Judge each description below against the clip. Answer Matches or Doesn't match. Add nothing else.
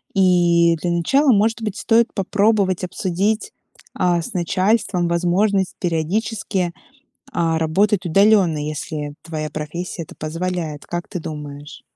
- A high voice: Doesn't match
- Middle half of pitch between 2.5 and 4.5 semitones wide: Matches